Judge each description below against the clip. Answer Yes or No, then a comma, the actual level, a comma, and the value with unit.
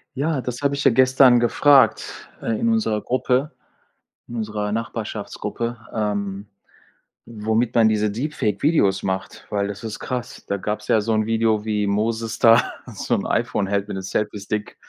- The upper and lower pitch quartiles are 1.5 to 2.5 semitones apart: No, average, 2.9 semitones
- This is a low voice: Yes, low, 110 Hz